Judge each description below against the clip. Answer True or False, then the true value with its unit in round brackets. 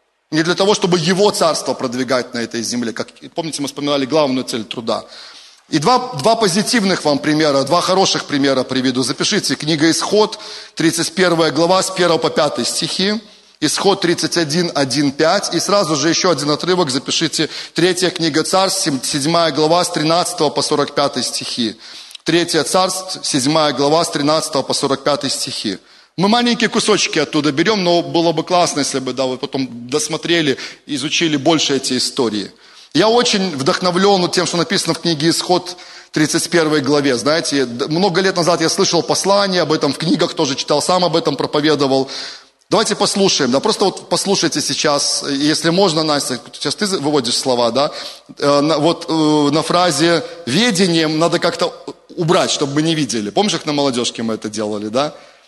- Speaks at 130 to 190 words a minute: True (160 wpm)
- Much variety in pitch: False (3.9 semitones)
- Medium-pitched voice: True (165 Hz)